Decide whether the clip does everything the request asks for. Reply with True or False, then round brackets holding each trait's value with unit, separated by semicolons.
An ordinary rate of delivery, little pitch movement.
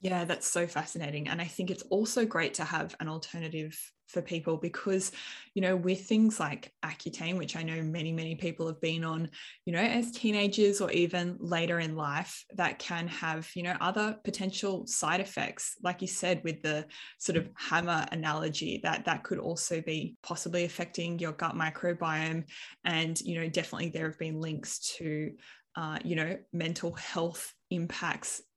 True (175 wpm; 2.3 semitones)